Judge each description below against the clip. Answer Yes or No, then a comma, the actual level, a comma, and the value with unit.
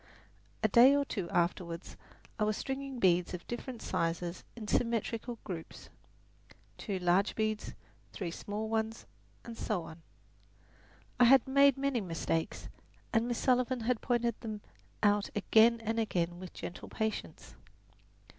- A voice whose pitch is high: Yes, high, 220 Hz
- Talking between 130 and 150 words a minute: Yes, slow, 135 wpm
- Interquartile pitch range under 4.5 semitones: No, average, 4.8 semitones